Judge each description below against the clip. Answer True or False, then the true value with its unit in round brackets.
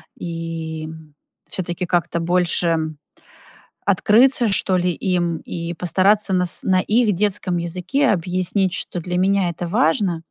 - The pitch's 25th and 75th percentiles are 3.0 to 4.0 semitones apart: False (2.6 semitones)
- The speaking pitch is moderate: True (180 Hz)